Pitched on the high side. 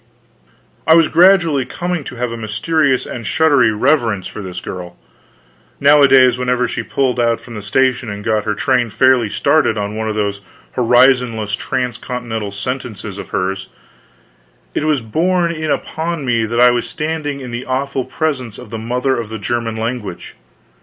No: low, 125 Hz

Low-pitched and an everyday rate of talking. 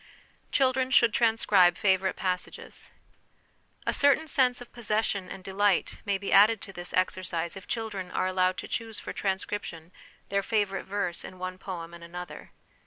No: high, 195 Hz; average, 165 wpm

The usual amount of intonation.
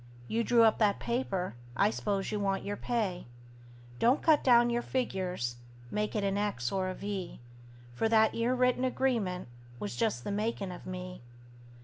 Yes: average, 4.2 semitones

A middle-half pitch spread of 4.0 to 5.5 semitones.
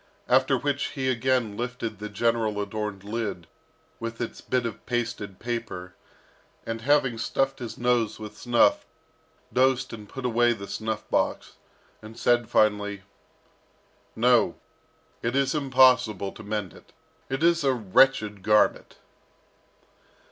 No: average, 3.2 semitones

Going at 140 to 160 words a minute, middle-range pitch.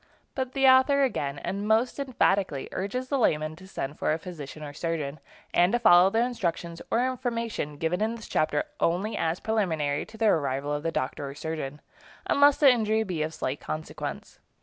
No: average, 190 wpm; medium, 180 Hz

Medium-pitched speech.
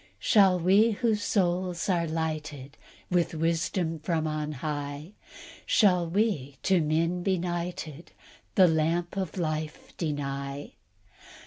Yes: medium, 165 Hz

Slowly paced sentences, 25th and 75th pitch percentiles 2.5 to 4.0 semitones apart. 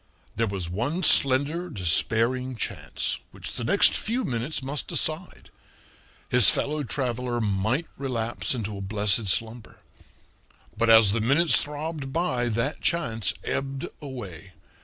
No: slow, 130 wpm; average, 4.5 semitones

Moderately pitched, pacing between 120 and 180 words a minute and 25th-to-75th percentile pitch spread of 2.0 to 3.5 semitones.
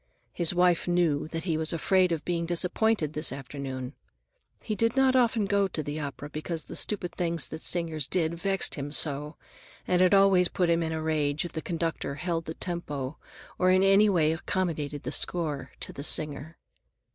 No: medium, 165 Hz; average, 190 wpm; average, 3.1 semitones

